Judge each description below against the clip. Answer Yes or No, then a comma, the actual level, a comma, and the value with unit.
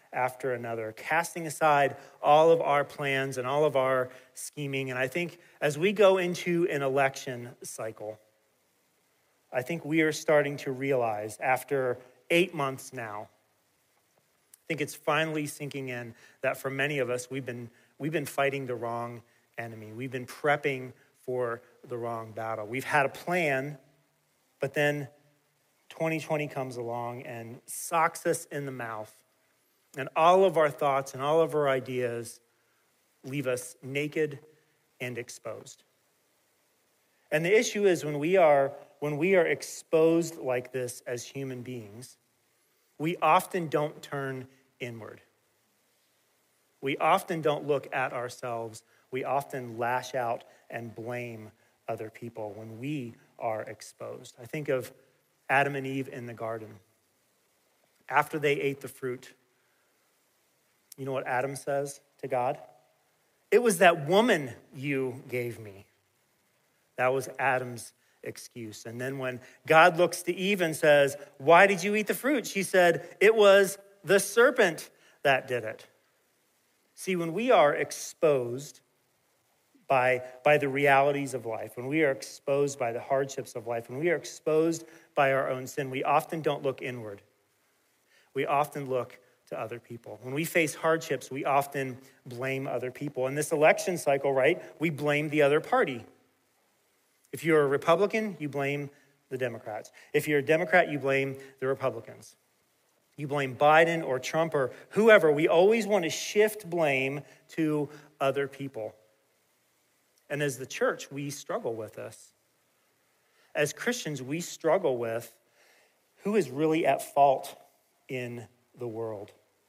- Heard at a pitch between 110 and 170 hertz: Yes, medium, 140 Hz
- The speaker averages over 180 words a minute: No, average, 150 wpm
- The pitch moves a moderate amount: Yes, average, 3.8 semitones